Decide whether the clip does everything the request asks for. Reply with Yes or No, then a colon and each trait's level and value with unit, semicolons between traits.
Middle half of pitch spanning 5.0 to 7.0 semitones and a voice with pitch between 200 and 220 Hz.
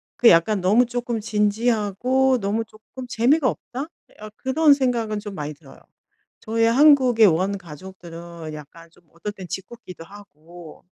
Yes: wide, 5.6 semitones; high, 210 Hz